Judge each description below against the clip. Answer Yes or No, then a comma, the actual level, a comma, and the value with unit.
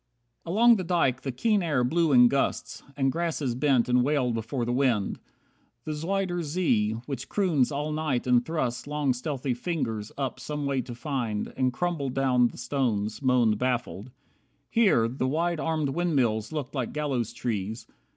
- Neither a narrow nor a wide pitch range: Yes, average, 4.1 semitones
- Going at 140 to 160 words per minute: No, average, 170 wpm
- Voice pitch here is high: No, low, 135 Hz